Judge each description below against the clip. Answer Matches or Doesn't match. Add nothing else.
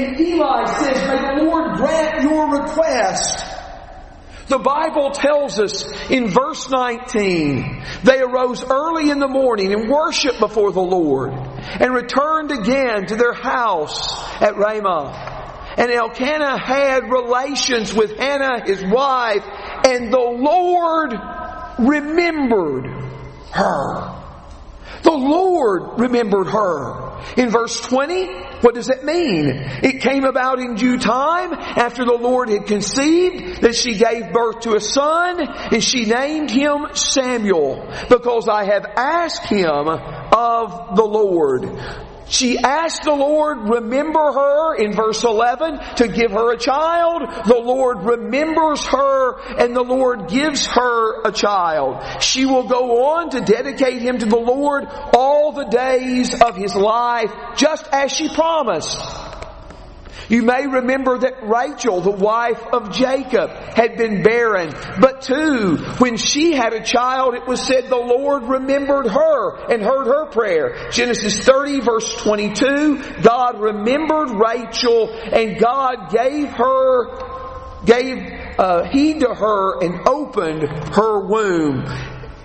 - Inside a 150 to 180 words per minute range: Doesn't match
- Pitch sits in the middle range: Doesn't match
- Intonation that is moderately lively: Matches